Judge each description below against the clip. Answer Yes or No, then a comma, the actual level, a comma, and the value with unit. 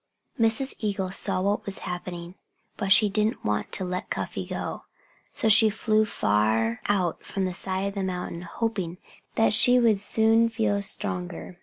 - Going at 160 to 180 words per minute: Yes, average, 165 wpm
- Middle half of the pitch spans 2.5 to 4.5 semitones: Yes, average, 3.5 semitones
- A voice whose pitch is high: Yes, high, 195 Hz